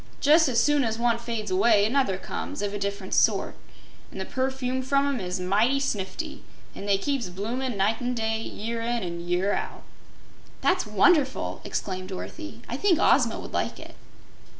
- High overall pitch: Yes, high, 230 Hz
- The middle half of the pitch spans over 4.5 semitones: Yes, average, 4.9 semitones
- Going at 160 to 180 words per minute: Yes, average, 175 wpm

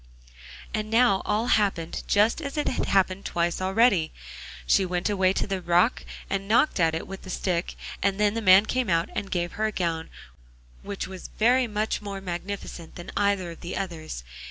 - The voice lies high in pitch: Yes, high, 195 Hz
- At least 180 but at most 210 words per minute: Yes, average, 190 wpm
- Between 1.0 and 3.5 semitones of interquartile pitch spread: Yes, average, 3.2 semitones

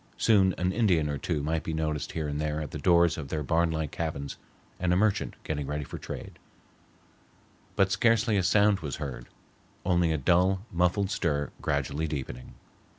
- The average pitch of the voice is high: No, very low, 80 Hz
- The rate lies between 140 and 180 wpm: Yes, average, 175 wpm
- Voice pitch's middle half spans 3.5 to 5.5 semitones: Yes, average, 4.0 semitones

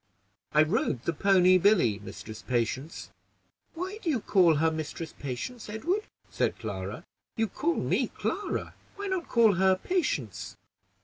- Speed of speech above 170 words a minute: No, average, 140 wpm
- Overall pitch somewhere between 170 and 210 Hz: Yes, medium, 185 Hz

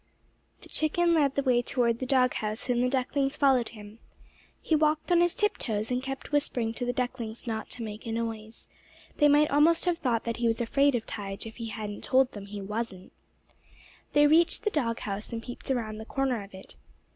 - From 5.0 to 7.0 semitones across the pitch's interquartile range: No, average, 4.1 semitones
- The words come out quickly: Yes, fast, 215 wpm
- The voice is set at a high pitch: Yes, high, 245 Hz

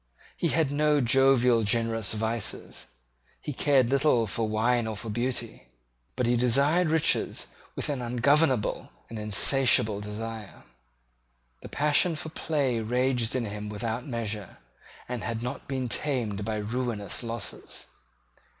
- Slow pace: Yes, slow, 130 wpm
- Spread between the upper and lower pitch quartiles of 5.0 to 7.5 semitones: No, average, 3.4 semitones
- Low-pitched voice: Yes, low, 120 Hz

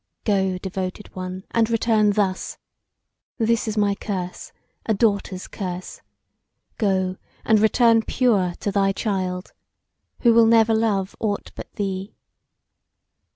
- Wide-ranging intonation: No, average, 2.8 semitones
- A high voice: Yes, high, 205 Hz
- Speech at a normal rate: No, slow, 120 wpm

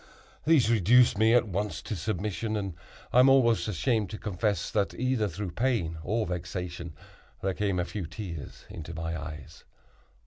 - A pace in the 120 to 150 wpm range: No, average, 165 wpm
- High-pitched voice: No, low, 100 Hz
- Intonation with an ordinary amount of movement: Yes, average, 4.8 semitones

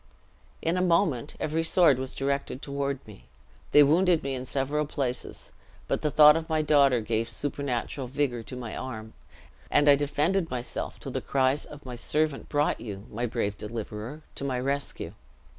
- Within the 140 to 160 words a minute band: No, average, 175 wpm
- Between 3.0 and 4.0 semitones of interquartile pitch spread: Yes, average, 3.3 semitones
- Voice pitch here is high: No, medium, 140 Hz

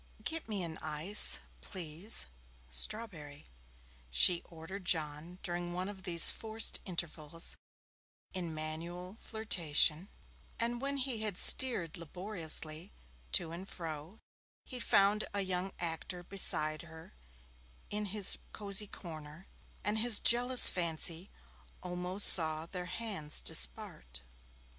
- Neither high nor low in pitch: Yes, medium, 180 Hz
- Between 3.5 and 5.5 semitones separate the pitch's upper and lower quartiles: Yes, average, 4.4 semitones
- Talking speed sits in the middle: No, slow, 115 wpm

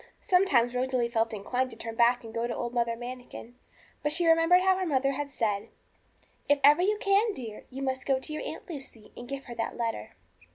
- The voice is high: Yes, very high, 255 Hz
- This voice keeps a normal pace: No, fast, 215 wpm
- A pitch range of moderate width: Yes, average, 4.1 semitones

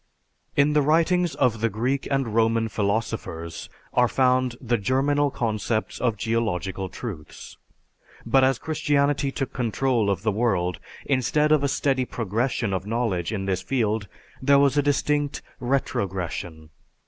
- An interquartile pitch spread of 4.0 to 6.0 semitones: Yes, average, 4.9 semitones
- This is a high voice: No, low, 120 Hz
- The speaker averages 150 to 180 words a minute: No, average, 140 wpm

